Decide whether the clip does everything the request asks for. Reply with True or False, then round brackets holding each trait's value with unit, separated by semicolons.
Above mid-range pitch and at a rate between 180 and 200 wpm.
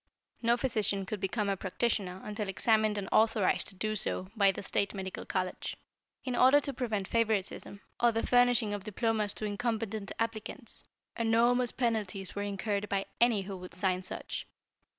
False (215 Hz; 165 wpm)